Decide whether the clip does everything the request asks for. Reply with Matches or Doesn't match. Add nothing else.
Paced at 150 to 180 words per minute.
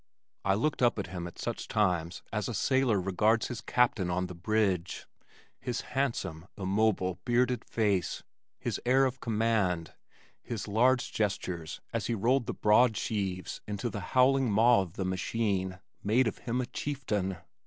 Matches